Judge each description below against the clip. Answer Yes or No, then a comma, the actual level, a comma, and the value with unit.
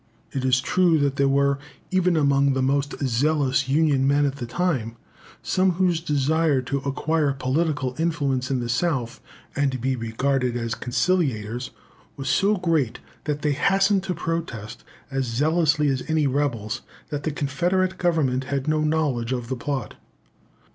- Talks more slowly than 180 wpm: Yes, average, 155 wpm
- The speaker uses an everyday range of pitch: Yes, average, 3.6 semitones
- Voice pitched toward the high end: No, medium, 140 Hz